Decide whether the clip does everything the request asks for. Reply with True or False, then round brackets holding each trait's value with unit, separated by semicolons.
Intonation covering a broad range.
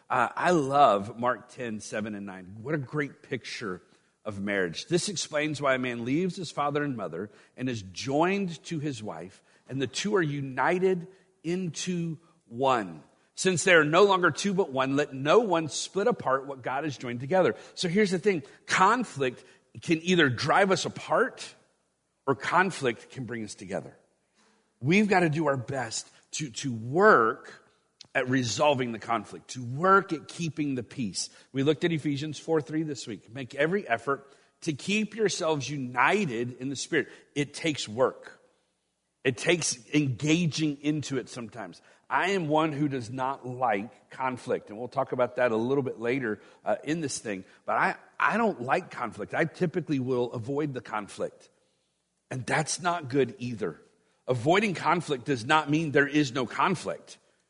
False (5.0 semitones)